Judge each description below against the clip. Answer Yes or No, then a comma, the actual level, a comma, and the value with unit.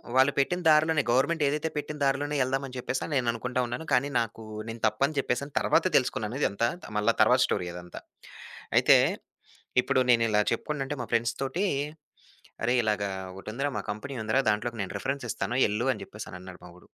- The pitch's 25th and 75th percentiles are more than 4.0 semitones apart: Yes, average, 4.4 semitones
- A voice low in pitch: Yes, low, 125 Hz